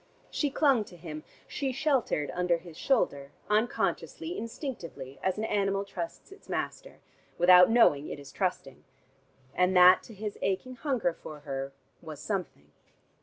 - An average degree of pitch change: No, wide, 7.2 semitones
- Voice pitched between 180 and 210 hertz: Yes, medium, 185 Hz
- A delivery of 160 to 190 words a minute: No, average, 145 wpm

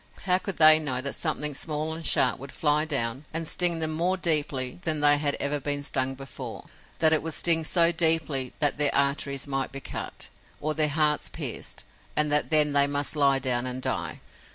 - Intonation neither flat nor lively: No, narrow, 2.3 semitones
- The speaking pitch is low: No, medium, 150 Hz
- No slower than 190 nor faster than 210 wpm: Yes, average, 200 wpm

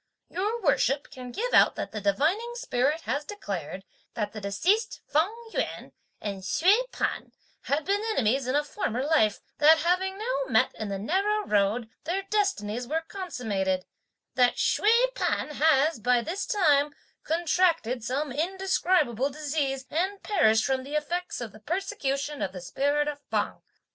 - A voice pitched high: Yes, very high, 295 Hz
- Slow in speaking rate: No, average, 155 wpm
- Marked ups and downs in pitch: Yes, wide, 7.6 semitones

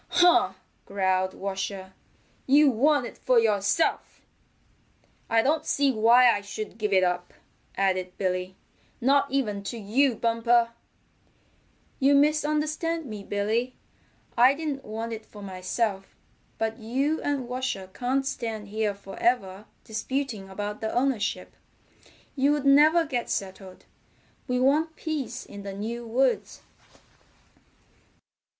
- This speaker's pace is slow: Yes, slow, 120 wpm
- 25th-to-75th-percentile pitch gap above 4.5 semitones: Yes, average, 5.3 semitones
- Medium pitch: No, high, 230 Hz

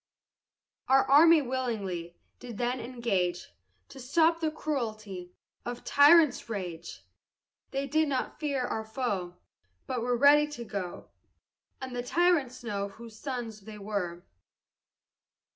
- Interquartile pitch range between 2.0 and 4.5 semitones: No, average, 5.3 semitones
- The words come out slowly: Yes, slow, 125 wpm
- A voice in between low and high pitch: No, high, 245 Hz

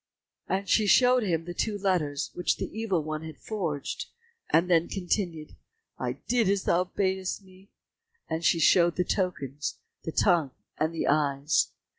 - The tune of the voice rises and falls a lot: No, average, 3.6 semitones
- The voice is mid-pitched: Yes, medium, 175 Hz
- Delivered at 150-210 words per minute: Yes, average, 155 wpm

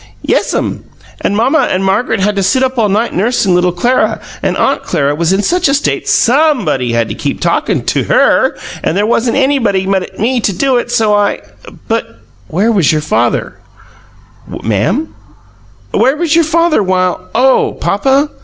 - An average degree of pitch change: No, wide, 6.1 semitones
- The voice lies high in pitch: Yes, high, 215 Hz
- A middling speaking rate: Yes, average, 185 wpm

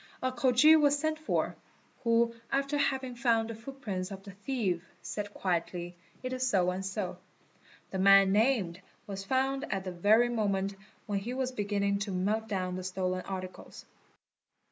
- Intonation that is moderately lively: Yes, average, 4.9 semitones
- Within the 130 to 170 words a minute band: Yes, average, 165 wpm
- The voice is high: Yes, high, 205 Hz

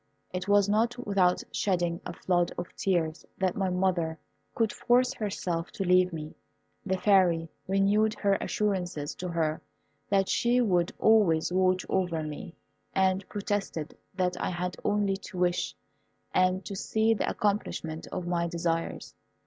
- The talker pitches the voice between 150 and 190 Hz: Yes, medium, 185 Hz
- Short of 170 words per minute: Yes, average, 150 wpm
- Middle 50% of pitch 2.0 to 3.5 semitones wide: Yes, average, 2.7 semitones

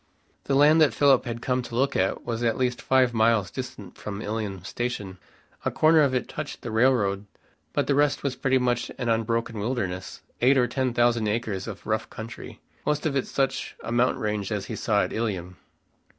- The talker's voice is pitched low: Yes, low, 120 Hz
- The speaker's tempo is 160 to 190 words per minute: No, average, 200 wpm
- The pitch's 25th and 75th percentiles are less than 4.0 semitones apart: Yes, average, 3.6 semitones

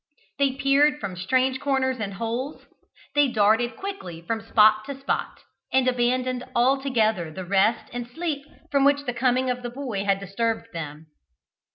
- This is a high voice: Yes, high, 245 Hz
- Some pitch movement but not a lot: Yes, average, 4.0 semitones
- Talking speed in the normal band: Yes, average, 160 wpm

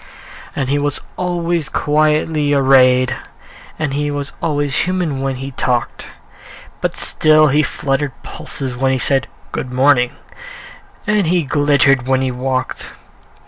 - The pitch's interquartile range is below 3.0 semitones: Yes, narrow, 2.4 semitones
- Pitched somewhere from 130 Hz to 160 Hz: Yes, medium, 140 Hz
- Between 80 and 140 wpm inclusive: Yes, slow, 135 wpm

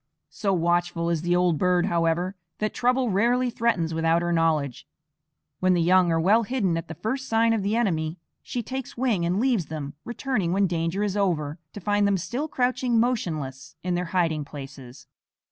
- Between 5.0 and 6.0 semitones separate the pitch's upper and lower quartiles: Yes, average, 5.3 semitones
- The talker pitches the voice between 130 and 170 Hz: No, medium, 180 Hz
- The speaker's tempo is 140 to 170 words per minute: No, average, 185 wpm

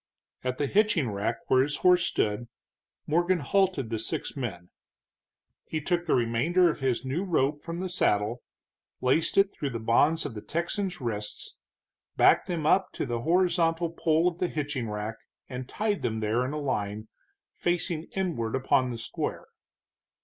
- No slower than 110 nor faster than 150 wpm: No, average, 165 wpm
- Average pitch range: No, wide, 6.9 semitones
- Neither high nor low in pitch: Yes, medium, 145 Hz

